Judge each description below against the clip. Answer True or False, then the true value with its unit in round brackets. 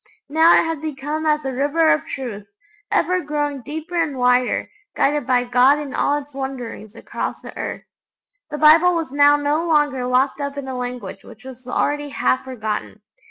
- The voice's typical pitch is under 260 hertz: False (285 Hz)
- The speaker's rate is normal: True (180 wpm)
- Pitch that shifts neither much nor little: True (3.0 semitones)